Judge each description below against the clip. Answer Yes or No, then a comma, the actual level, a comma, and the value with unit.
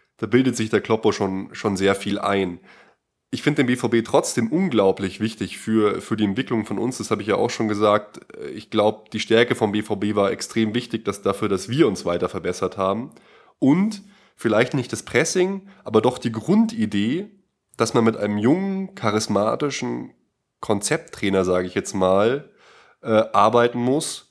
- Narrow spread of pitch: No, average, 3.8 semitones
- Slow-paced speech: No, average, 175 wpm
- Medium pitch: No, low, 110 Hz